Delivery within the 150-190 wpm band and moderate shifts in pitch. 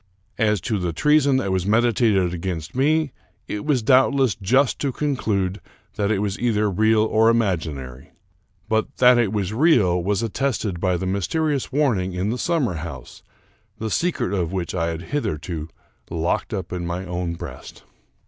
No: average, 170 wpm; wide, 5.7 semitones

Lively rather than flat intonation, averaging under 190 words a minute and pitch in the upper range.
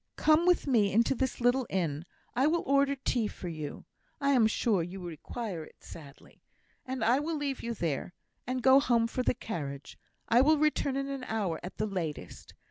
No: wide, 7.3 semitones; average, 195 wpm; high, 235 Hz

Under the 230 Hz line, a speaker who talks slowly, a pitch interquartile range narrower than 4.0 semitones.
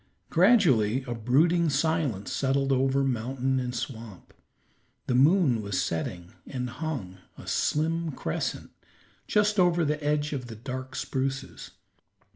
No: low, 135 Hz; slow, 125 wpm; average, 4.5 semitones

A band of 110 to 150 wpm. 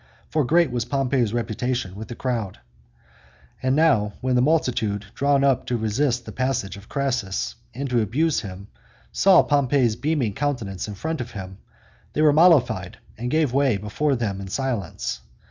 No: average, 165 wpm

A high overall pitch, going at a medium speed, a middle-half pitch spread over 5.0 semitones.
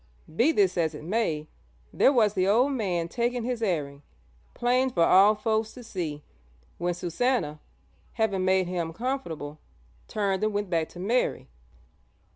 Yes: high, 195 Hz; average, 150 wpm; wide, 5.5 semitones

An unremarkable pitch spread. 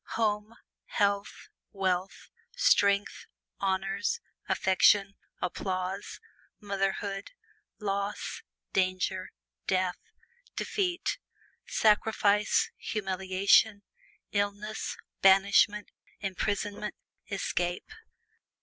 No: narrow, 1.5 semitones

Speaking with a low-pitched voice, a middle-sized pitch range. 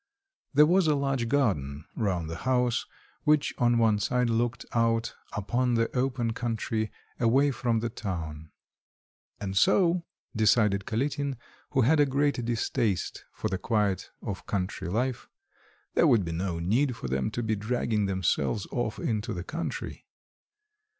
Yes: low, 115 Hz; average, 4.4 semitones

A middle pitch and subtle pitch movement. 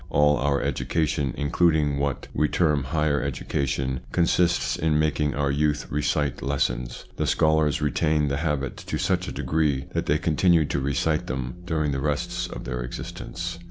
No: very low, 75 Hz; narrow, 2.0 semitones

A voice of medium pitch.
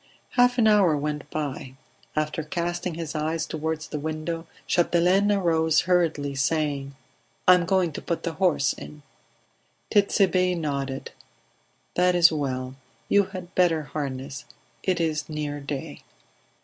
Yes: medium, 160 Hz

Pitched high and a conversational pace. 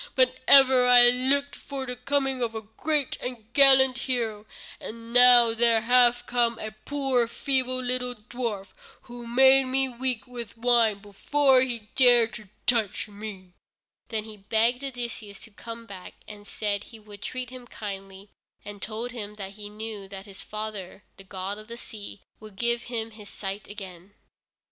Yes: high, 230 Hz; average, 170 wpm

